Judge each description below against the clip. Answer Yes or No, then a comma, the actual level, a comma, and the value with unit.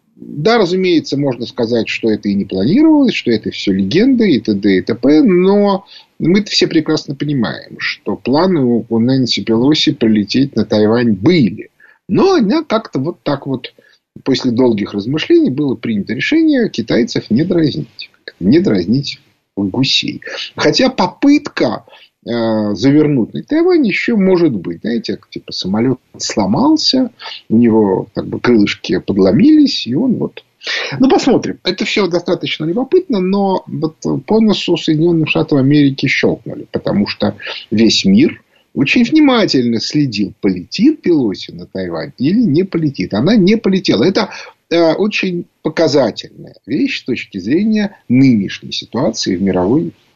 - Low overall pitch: No, medium, 160 Hz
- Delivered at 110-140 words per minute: Yes, average, 135 wpm